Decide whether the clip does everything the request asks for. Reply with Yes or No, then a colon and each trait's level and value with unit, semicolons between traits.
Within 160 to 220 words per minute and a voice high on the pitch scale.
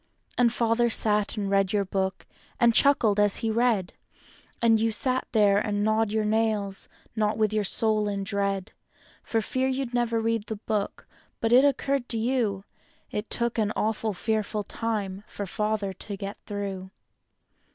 Yes: average, 165 wpm; high, 215 Hz